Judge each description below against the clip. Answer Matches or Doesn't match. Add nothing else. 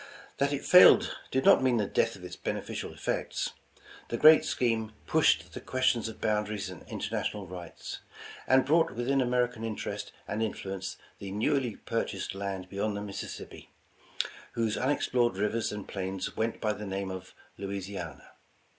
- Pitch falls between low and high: Doesn't match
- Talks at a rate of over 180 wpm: Doesn't match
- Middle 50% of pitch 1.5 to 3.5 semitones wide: Doesn't match